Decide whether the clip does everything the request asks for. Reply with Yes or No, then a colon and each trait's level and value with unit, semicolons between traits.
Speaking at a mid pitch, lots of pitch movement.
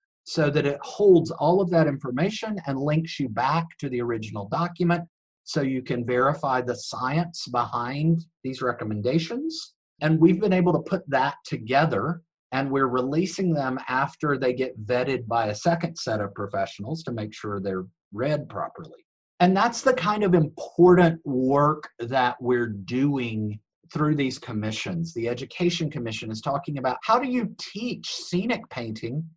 Yes: medium, 145 Hz; wide, 5.7 semitones